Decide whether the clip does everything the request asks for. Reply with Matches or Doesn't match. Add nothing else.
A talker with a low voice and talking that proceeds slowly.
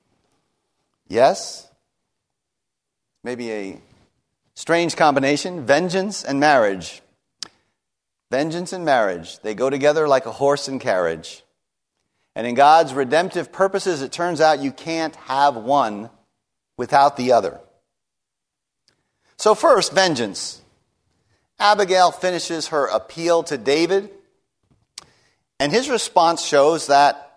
Doesn't match